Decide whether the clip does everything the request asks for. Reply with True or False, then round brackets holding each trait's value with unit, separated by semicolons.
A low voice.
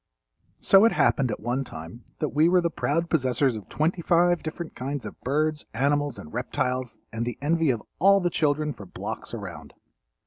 False (145 Hz)